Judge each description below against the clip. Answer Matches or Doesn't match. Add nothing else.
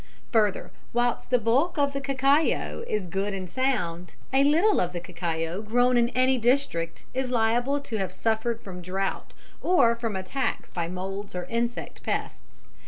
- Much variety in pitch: Matches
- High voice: Matches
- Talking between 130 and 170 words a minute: Matches